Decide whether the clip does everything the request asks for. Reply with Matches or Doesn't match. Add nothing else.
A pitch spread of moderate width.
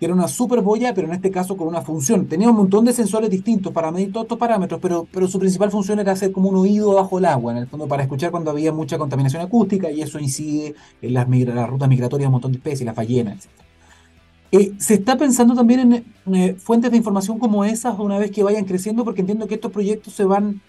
Doesn't match